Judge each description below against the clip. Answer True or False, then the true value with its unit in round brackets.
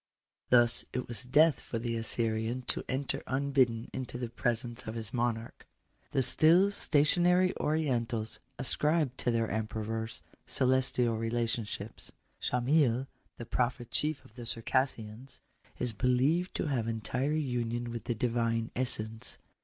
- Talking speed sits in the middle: False (130 wpm)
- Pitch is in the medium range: False (120 Hz)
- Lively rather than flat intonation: False (2.7 semitones)